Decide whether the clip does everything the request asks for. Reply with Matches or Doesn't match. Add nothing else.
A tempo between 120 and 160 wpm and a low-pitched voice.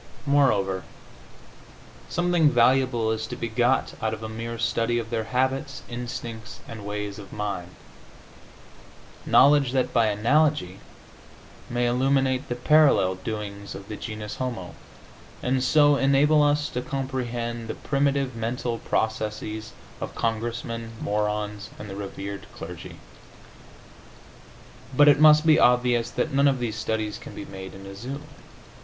Matches